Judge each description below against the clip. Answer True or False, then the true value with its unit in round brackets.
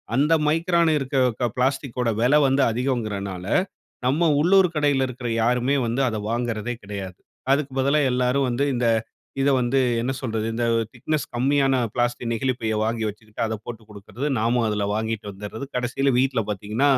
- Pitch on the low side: True (125 Hz)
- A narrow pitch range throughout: False (3.6 semitones)